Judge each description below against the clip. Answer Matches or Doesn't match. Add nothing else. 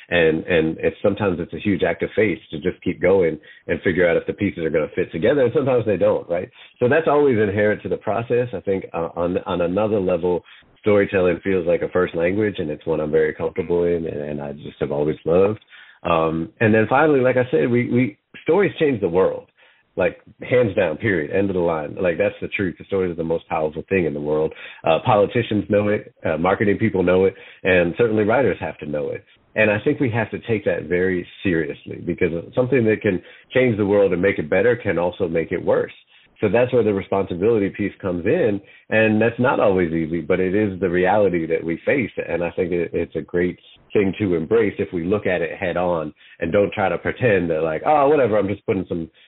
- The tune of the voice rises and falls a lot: Matches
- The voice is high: Doesn't match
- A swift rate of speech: Matches